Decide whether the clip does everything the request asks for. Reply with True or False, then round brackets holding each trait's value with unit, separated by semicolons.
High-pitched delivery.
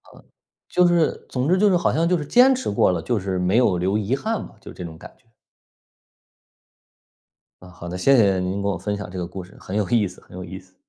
False (100 Hz)